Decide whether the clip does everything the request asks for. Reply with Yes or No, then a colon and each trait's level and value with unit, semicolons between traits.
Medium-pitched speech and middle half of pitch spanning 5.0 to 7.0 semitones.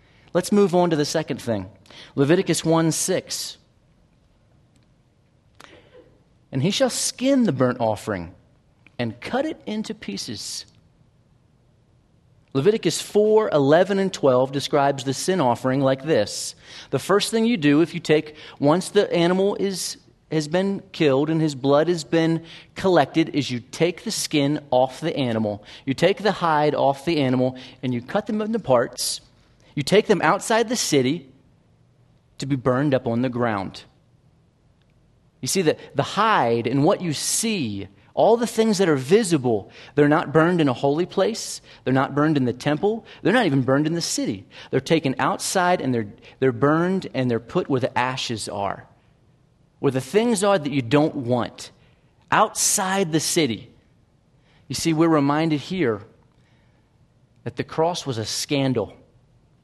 Yes: medium, 145 Hz; wide, 5.6 semitones